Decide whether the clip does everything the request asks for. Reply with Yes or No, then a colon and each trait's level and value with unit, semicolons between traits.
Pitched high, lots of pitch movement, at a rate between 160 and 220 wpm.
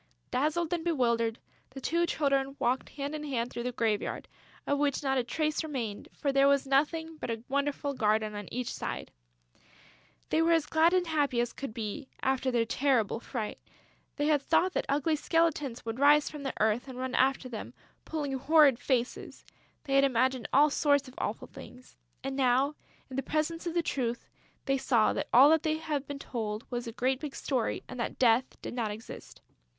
No: very high, 270 Hz; average, 3.6 semitones; average, 195 wpm